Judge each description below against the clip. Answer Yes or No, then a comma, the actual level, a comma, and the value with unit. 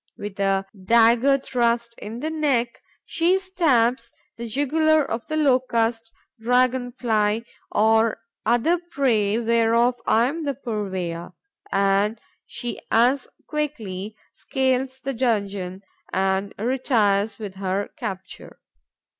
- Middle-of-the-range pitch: No, high, 235 Hz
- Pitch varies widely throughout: No, average, 4.0 semitones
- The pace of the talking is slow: Yes, slow, 115 wpm